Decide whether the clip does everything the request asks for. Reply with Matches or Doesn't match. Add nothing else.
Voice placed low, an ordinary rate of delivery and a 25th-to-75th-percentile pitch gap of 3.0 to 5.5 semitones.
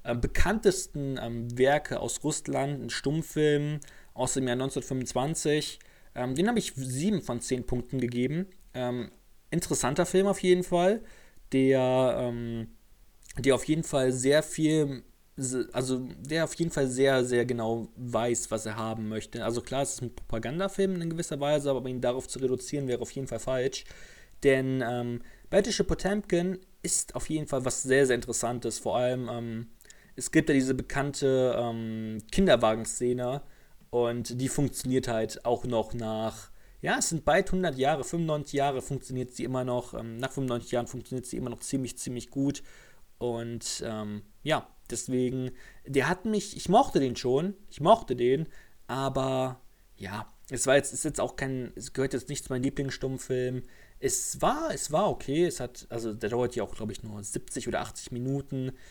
Matches